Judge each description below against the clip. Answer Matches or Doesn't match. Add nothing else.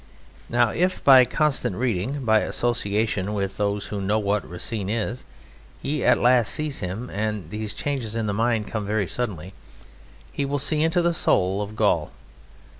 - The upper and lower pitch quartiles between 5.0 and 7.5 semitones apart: Doesn't match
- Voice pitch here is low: Matches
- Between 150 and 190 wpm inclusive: Matches